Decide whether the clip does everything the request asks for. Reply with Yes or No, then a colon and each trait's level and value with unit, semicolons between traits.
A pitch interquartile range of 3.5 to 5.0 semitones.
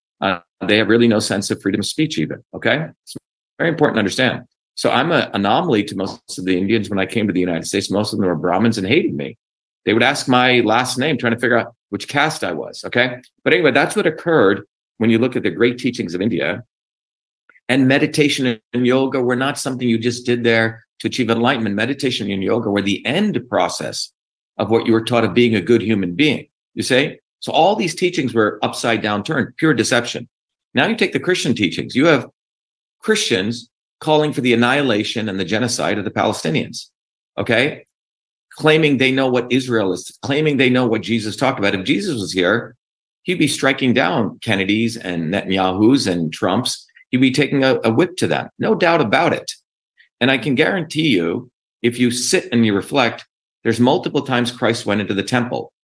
Yes: average, 3.8 semitones